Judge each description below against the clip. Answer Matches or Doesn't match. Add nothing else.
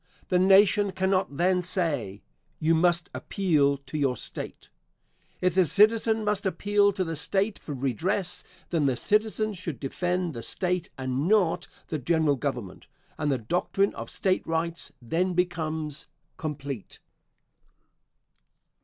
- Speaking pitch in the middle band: Matches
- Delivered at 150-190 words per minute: Doesn't match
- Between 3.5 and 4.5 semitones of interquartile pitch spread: Doesn't match